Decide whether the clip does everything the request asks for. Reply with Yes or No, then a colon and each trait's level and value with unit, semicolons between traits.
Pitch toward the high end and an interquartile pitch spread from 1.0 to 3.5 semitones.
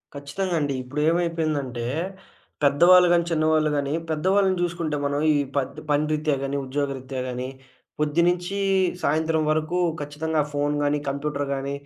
No: medium, 150 Hz; narrow, 2.6 semitones